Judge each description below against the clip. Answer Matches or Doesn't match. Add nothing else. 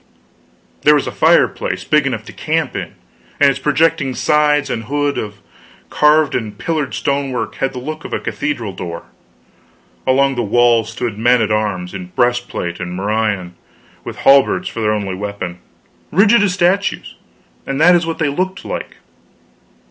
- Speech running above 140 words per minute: Matches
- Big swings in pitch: Matches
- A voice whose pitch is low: Matches